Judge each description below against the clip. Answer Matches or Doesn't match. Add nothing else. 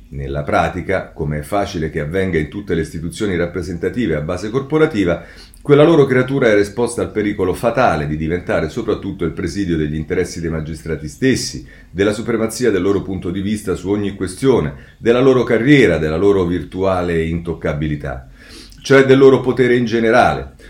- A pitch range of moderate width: Doesn't match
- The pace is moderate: Matches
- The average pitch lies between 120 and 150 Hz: Doesn't match